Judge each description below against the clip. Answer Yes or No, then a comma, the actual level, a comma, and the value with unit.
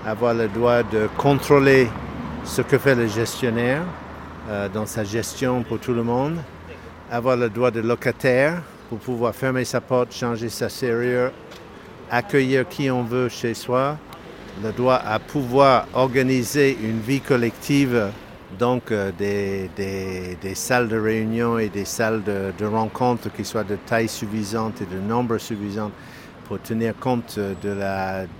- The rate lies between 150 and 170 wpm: Yes, average, 155 wpm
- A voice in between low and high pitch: No, low, 115 Hz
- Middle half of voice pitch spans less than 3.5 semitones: Yes, average, 3.1 semitones